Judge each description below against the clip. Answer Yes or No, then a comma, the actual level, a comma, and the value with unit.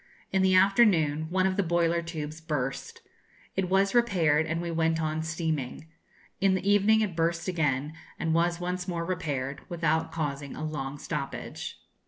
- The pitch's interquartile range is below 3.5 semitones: Yes, average, 3.0 semitones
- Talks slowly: No, average, 165 wpm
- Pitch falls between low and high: Yes, medium, 165 Hz